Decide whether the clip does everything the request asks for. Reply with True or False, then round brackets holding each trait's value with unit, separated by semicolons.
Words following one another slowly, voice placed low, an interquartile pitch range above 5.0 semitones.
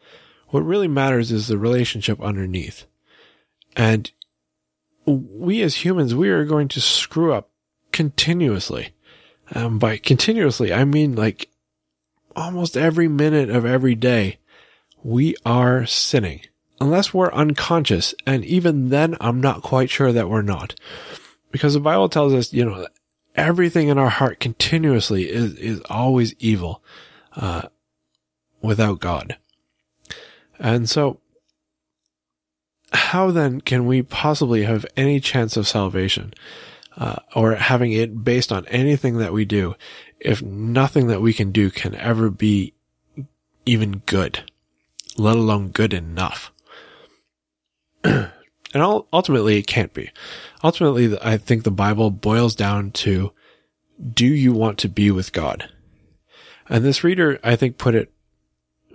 True (130 wpm; 115 Hz; 5.5 semitones)